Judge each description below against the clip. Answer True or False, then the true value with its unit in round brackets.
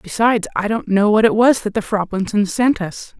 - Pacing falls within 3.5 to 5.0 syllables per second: False (5.2 syllables/s)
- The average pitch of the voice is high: True (210 Hz)